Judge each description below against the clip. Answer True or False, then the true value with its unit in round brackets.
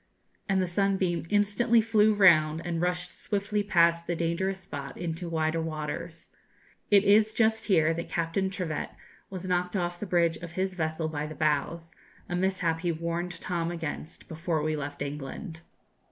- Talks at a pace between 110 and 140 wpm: False (165 wpm)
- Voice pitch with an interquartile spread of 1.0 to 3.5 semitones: True (2.9 semitones)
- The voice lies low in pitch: False (170 Hz)